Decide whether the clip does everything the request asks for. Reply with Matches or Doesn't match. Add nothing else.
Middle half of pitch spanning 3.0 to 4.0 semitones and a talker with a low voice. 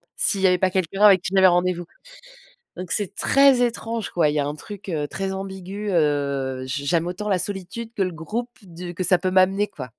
Doesn't match